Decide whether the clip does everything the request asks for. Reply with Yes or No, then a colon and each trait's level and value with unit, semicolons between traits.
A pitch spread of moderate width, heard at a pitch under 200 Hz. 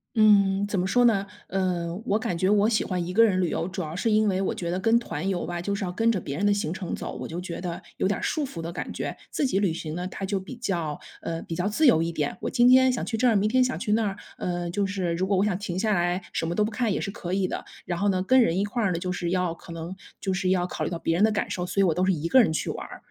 Yes: average, 3.2 semitones; high, 190 Hz